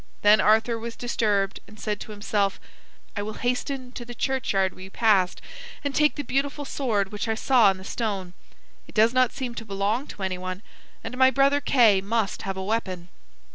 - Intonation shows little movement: No, average, 4.1 semitones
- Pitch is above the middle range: Yes, high, 220 Hz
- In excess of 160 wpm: Yes, average, 190 wpm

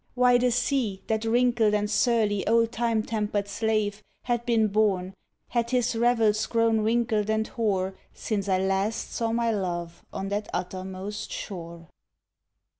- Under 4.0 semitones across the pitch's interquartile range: Yes, average, 2.7 semitones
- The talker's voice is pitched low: No, high, 215 Hz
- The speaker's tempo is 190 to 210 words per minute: No, average, 145 wpm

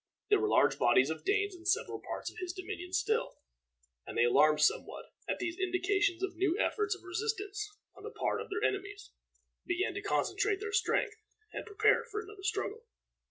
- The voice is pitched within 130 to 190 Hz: No, very high, 400 Hz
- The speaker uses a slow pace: No, average, 185 wpm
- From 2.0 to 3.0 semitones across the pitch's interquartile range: Yes, narrow, 2.6 semitones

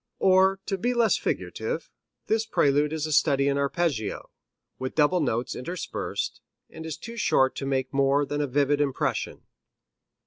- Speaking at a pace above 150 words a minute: Yes, average, 160 wpm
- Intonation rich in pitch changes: No, average, 4.7 semitones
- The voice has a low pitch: No, medium, 145 Hz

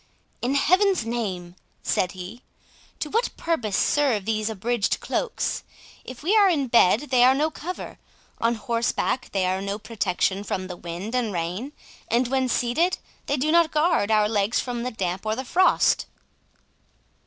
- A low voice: No, high, 235 Hz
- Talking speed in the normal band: Yes, average, 165 wpm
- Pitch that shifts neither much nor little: No, wide, 5.8 semitones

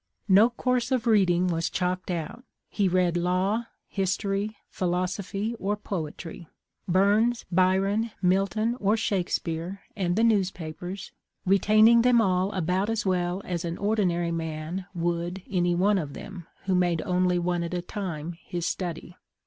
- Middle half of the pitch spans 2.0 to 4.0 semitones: Yes, average, 2.8 semitones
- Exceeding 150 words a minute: No, average, 145 wpm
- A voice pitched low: No, medium, 185 Hz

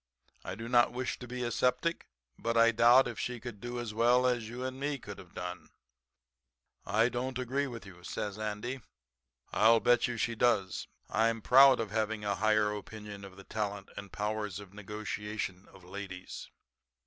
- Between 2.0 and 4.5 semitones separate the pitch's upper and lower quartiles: Yes, average, 3.0 semitones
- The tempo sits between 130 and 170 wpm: No, average, 185 wpm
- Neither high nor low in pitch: No, low, 110 Hz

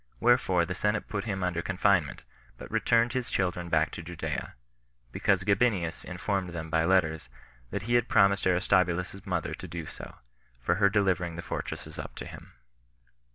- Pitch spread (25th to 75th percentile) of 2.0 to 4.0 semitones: Yes, average, 2.8 semitones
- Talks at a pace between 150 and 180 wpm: Yes, average, 165 wpm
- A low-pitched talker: Yes, very low, 90 Hz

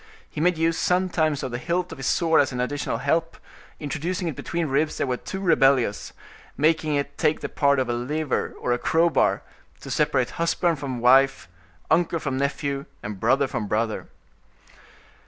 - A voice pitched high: No, medium, 145 Hz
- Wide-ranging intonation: No, average, 3.8 semitones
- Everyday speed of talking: Yes, average, 175 wpm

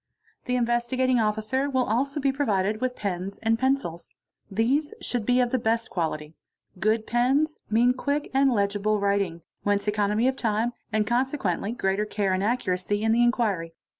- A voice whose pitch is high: Yes, high, 225 Hz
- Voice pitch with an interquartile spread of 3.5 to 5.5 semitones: Yes, average, 3.9 semitones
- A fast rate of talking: No, average, 170 wpm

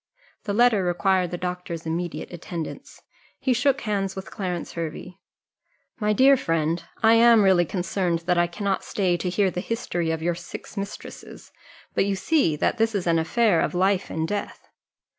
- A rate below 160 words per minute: No, average, 175 wpm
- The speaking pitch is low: No, medium, 185 Hz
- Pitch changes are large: No, average, 3.3 semitones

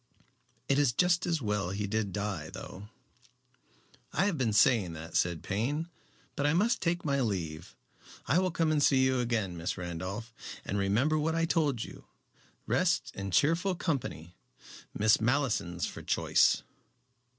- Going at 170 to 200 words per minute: No, average, 155 wpm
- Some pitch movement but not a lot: No, wide, 7.9 semitones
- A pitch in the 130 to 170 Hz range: No, low, 115 Hz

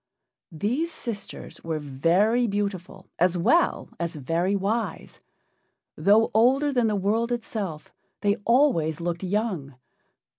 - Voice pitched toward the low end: No, high, 200 Hz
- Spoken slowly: Yes, slow, 115 wpm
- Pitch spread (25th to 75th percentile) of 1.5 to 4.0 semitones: No, average, 5.2 semitones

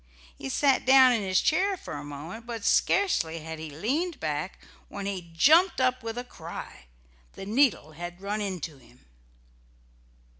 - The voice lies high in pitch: Yes, high, 200 Hz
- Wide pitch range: Yes, wide, 8.2 semitones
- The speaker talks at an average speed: Yes, average, 160 wpm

